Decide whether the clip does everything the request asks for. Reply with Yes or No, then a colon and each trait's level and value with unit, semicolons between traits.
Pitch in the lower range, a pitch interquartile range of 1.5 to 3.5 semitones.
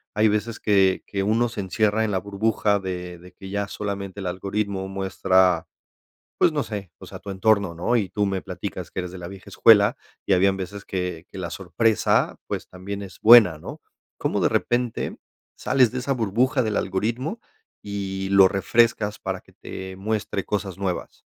Yes: low, 100 Hz; narrow, 2.5 semitones